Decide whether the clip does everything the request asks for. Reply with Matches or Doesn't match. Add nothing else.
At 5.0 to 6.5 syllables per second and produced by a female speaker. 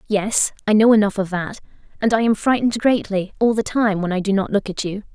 Matches